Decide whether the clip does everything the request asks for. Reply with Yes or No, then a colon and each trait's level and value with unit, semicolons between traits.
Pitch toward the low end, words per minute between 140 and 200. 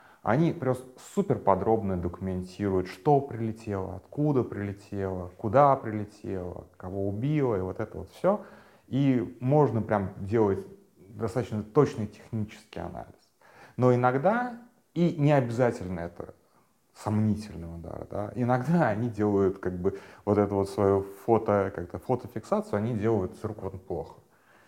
No: low, 110 Hz; average, 125 wpm